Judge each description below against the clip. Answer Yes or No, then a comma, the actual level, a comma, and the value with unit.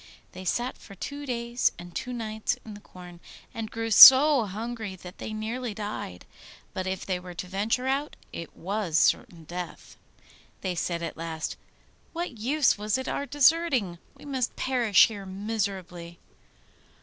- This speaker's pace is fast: No, average, 160 wpm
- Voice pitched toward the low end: No, high, 215 Hz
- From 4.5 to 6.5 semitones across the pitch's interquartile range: Yes, average, 5.3 semitones